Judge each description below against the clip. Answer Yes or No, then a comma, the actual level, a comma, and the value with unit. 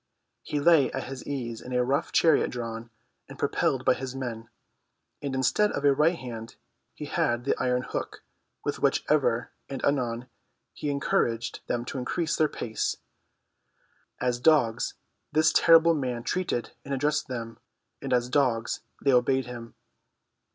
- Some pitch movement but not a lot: Yes, average, 3.2 semitones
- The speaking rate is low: No, average, 155 wpm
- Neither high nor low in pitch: No, low, 130 Hz